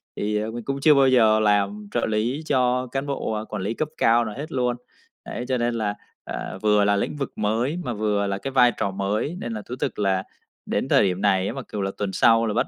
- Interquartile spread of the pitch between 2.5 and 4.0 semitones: Yes, average, 3.6 semitones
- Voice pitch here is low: Yes, low, 110 Hz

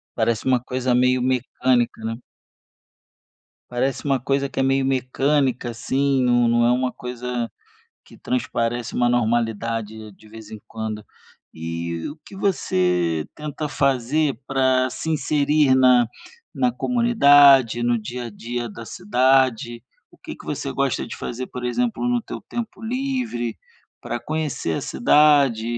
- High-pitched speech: No, low, 125 Hz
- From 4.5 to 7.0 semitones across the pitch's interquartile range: No, average, 3.3 semitones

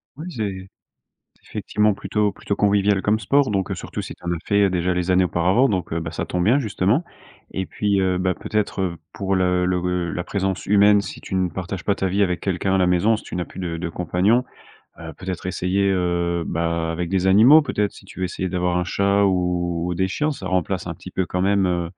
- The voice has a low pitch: Yes, very low, 95 Hz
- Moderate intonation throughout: No, narrow, 2.2 semitones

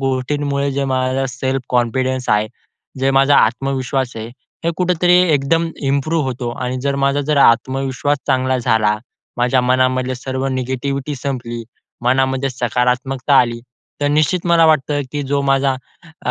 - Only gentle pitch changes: Yes, narrow, 1.7 semitones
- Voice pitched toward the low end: Yes, low, 130 Hz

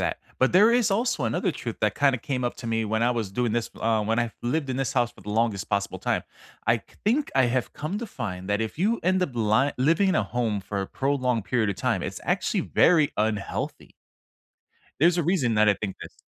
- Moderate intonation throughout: No, wide, 5.9 semitones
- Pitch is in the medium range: No, low, 120 Hz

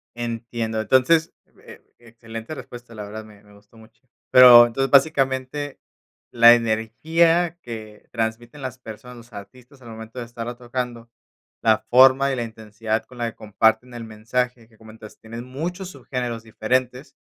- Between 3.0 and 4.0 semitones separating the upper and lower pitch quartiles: No, narrow, 2.5 semitones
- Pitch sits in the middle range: No, low, 120 Hz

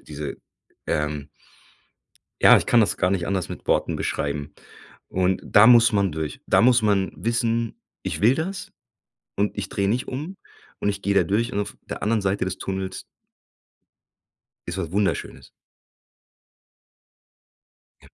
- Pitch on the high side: No, low, 100 Hz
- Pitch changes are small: No, average, 3.7 semitones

